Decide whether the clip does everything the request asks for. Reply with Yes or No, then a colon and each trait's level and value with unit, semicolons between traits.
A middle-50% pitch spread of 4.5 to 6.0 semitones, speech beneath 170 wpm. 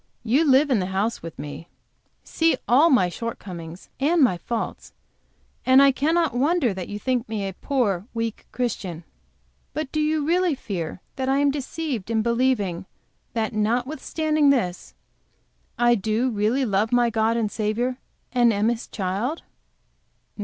Yes: average, 5.0 semitones; average, 155 wpm